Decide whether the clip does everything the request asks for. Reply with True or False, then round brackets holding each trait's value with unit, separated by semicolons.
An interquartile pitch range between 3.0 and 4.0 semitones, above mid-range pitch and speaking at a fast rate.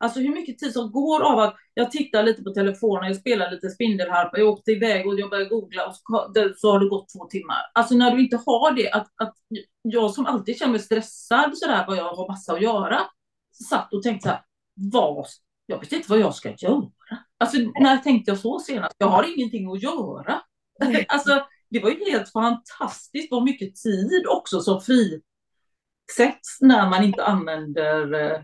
True (3.7 semitones; 220 Hz; 200 wpm)